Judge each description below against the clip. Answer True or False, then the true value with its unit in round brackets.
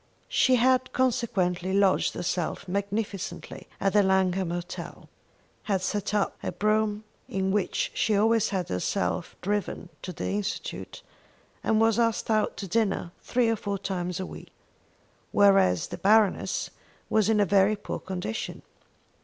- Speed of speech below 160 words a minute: True (145 wpm)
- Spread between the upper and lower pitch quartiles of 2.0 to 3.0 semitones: True (2.5 semitones)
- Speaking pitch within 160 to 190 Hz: False (200 Hz)